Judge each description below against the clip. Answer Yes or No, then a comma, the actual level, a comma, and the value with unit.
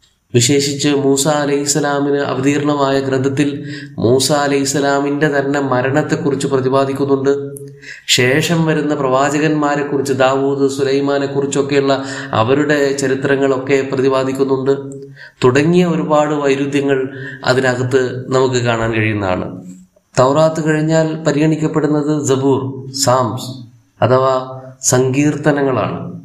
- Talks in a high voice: No, medium, 140 Hz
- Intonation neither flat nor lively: No, narrow, 1.6 semitones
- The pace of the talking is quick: No, average, 80 wpm